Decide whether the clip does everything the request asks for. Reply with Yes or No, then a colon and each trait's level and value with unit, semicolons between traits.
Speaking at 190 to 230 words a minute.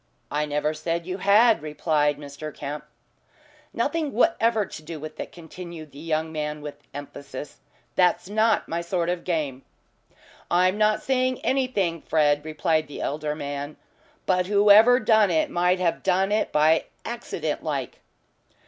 No: average, 150 wpm